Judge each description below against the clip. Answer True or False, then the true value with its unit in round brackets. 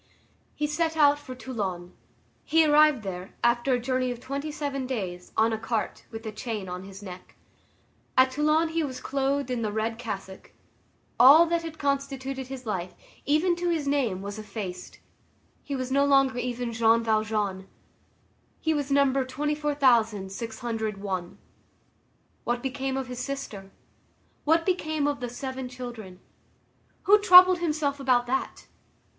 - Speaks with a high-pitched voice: True (255 Hz)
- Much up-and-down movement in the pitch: False (4.6 semitones)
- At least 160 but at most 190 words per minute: False (150 wpm)